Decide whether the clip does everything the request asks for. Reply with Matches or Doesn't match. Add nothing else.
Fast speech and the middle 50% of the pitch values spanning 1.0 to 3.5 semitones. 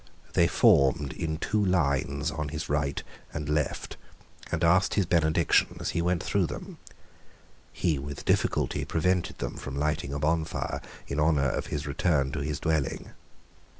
Doesn't match